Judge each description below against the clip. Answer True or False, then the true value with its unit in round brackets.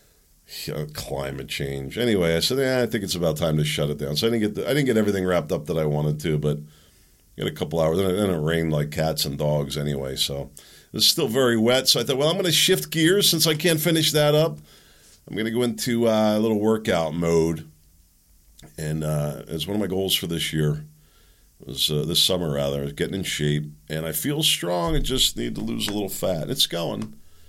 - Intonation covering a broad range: True (7.1 semitones)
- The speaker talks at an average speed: False (240 wpm)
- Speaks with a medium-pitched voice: False (80 Hz)